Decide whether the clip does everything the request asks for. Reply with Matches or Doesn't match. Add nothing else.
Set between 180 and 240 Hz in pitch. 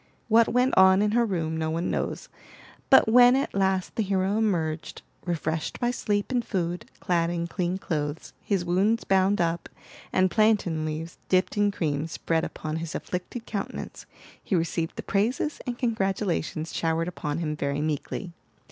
Matches